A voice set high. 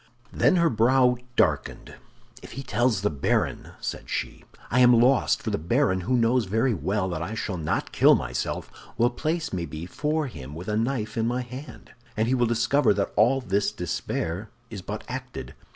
No: low, 115 Hz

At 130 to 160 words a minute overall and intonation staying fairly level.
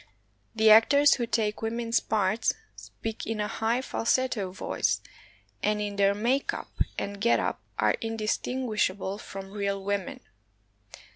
Yes: slow, 135 wpm; narrow, 2.3 semitones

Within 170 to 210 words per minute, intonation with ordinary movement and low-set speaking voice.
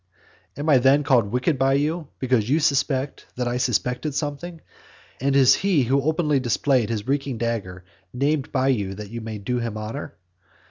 Yes: average, 180 wpm; average, 3.5 semitones; low, 130 Hz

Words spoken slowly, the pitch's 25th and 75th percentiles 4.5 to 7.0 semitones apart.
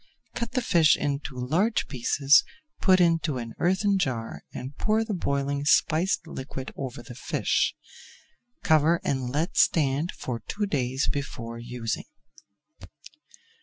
Yes: slow, 130 wpm; average, 5.3 semitones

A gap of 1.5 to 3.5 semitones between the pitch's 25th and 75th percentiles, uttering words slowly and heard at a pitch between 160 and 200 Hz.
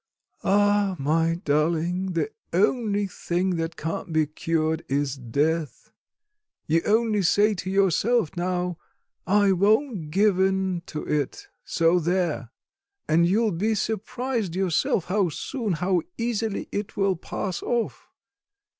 No: average, 3.9 semitones; slow, 130 wpm; medium, 185 Hz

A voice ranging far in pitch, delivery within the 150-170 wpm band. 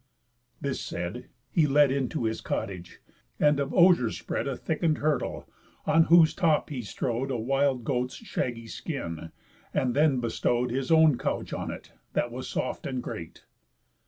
No: average, 3.9 semitones; average, 160 wpm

